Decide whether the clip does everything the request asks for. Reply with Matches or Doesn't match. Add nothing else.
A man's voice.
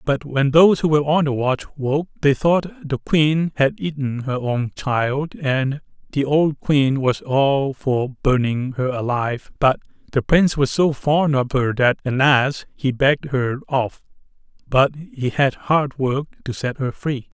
Matches